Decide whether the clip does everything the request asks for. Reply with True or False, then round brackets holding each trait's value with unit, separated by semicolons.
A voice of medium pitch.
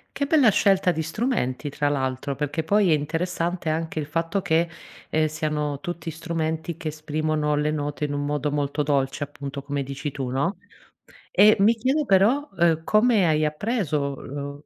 True (155 Hz)